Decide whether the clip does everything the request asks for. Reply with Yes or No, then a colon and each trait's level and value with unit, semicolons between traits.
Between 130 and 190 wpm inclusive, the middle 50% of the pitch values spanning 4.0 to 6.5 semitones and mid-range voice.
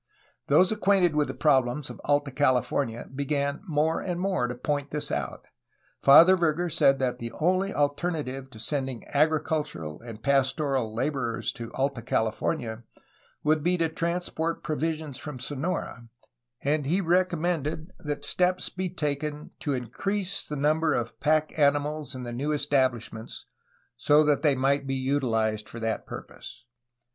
No: average, 150 wpm; average, 3.5 semitones; medium, 145 Hz